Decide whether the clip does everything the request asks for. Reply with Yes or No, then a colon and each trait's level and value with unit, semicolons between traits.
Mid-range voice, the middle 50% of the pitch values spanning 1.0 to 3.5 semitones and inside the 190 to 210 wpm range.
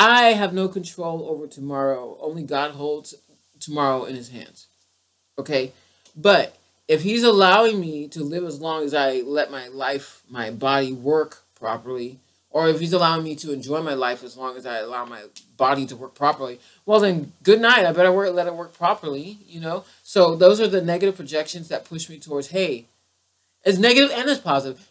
No: medium, 150 Hz; average, 5.3 semitones; average, 195 wpm